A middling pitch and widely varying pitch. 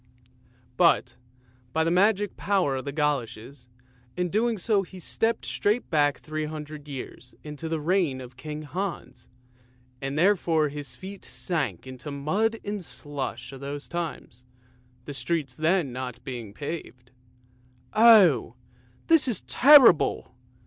Yes: medium, 155 Hz; wide, 5.8 semitones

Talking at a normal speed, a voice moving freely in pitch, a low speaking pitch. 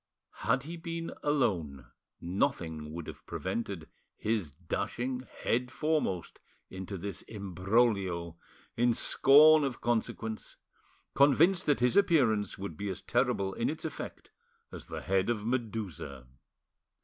No: slow, 125 wpm; wide, 5.8 semitones; low, 110 Hz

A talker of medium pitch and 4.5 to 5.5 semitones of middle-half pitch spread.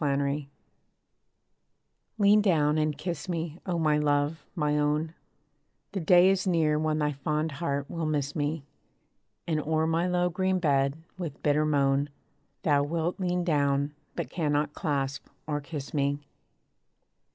No: medium, 150 Hz; narrow, 2.5 semitones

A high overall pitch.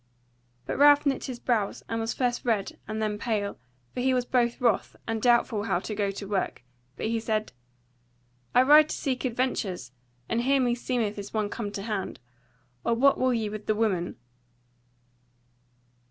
Yes: high, 225 Hz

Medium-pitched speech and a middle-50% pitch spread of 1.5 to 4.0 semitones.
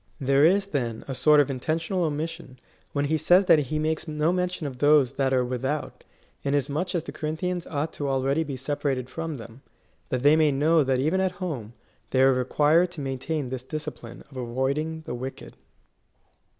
Yes: medium, 145 Hz; average, 3.4 semitones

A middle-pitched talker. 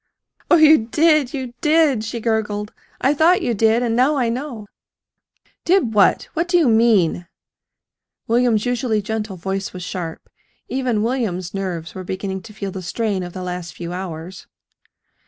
No: high, 220 Hz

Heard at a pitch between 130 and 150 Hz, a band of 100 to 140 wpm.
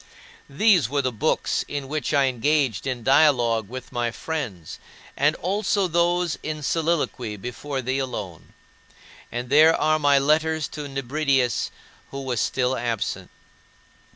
Yes: medium, 140 Hz; slow, 135 wpm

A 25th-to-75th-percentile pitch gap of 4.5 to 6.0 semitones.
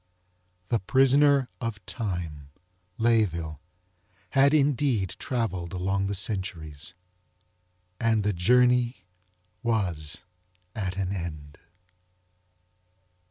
Yes: wide, 5.6 semitones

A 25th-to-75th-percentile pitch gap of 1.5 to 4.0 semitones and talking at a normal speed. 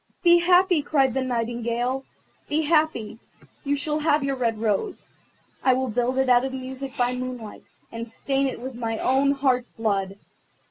Yes: average, 2.9 semitones; average, 170 wpm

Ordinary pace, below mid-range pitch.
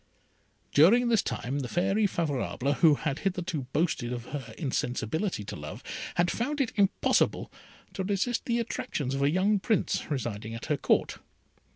No: average, 160 wpm; medium, 165 Hz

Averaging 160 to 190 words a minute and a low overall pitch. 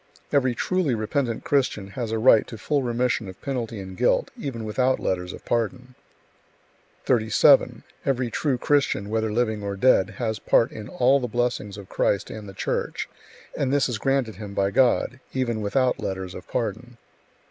Yes: average, 170 wpm; low, 115 Hz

